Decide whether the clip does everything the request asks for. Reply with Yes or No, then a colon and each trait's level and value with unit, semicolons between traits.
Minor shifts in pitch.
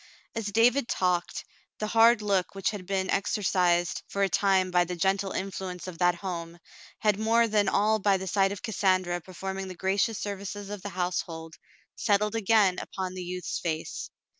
Yes: narrow, 2.3 semitones